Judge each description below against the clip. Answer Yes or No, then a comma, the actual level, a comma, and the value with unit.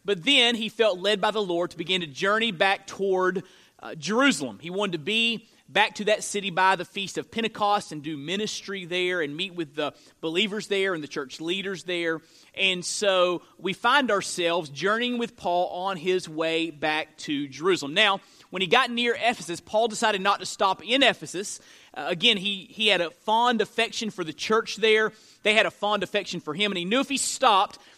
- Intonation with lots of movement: No, average, 3.5 semitones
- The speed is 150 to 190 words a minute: No, fast, 205 wpm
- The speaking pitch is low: No, high, 195 Hz